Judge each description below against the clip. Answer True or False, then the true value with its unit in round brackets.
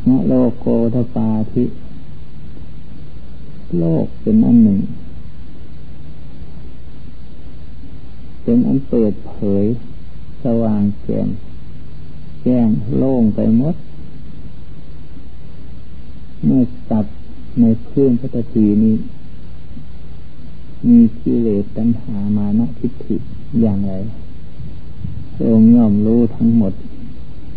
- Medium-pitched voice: False (110 Hz)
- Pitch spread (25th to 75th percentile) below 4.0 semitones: False (5.2 semitones)